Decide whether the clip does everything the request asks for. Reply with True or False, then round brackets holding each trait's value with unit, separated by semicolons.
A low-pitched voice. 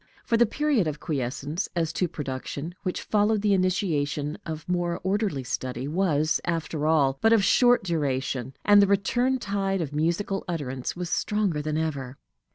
False (170 Hz)